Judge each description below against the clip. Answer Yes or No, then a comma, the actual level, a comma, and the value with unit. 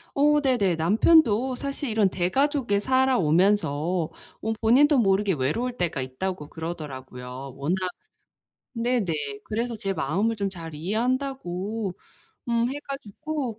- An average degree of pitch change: No, wide, 7.4 semitones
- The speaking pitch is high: Yes, high, 205 Hz